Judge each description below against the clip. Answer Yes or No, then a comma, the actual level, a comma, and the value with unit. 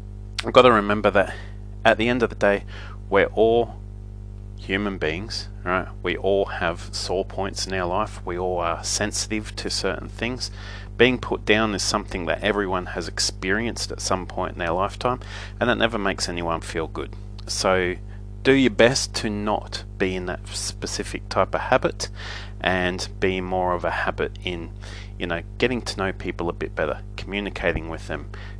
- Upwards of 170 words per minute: Yes, average, 180 wpm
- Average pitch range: No, narrow, 1.7 semitones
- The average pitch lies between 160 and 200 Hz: No, low, 100 Hz